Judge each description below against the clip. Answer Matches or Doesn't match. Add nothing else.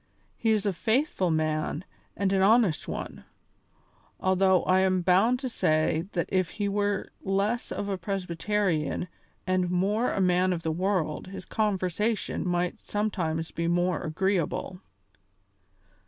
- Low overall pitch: Doesn't match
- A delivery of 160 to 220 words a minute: Doesn't match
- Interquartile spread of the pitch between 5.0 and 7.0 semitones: Doesn't match